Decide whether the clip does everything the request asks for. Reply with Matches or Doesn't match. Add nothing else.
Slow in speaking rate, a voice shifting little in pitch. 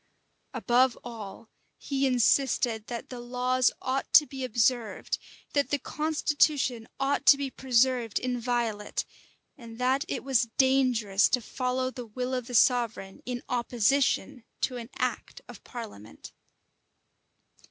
Matches